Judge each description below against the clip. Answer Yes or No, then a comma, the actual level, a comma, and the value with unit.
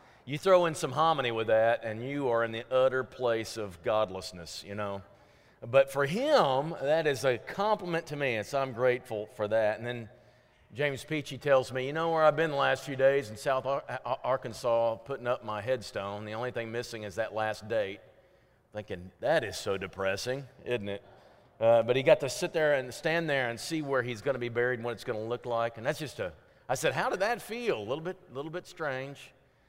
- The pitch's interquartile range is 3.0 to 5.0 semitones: Yes, average, 4.1 semitones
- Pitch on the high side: No, low, 125 Hz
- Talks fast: Yes, fast, 230 wpm